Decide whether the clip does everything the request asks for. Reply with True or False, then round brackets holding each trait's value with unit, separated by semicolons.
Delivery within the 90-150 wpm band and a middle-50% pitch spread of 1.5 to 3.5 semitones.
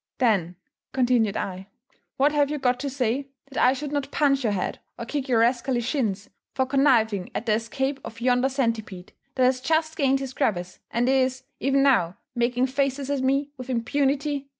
False (185 wpm; 3.1 semitones)